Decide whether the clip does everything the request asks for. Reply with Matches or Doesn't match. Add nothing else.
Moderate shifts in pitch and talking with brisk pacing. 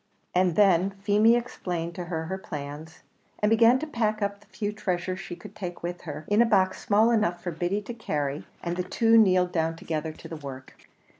Matches